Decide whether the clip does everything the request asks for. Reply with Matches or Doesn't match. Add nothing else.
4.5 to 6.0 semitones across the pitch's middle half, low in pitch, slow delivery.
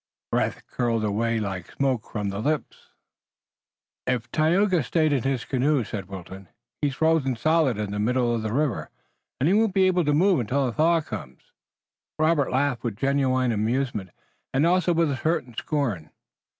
Doesn't match